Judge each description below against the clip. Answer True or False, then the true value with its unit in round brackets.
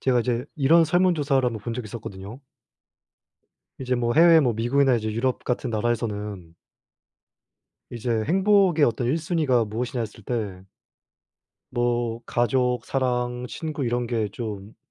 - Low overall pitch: True (120 Hz)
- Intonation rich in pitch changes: False (3.1 semitones)